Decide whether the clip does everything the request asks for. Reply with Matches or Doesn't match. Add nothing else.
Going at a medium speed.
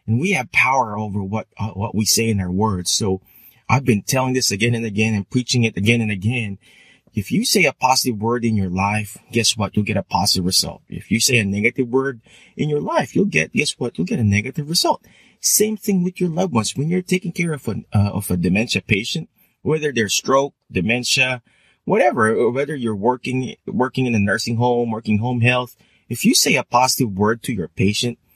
Doesn't match